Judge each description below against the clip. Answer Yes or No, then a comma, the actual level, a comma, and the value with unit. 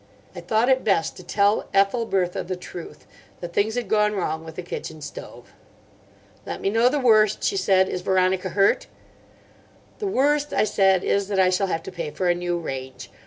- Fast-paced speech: No, average, 195 wpm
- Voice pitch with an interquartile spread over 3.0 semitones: Yes, average, 3.6 semitones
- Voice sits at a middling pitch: No, high, 195 Hz